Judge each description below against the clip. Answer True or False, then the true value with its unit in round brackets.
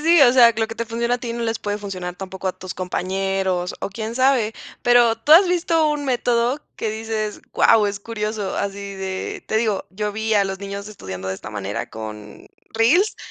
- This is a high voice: True (215 Hz)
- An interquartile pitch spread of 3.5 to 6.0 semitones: True (3.8 semitones)